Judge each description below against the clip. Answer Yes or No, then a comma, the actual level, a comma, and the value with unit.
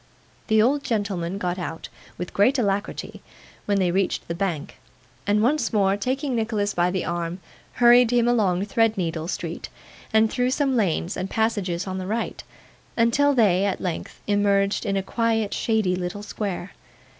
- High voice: Yes, high, 205 Hz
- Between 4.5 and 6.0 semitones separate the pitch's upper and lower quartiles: No, average, 3.8 semitones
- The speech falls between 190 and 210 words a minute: No, average, 160 wpm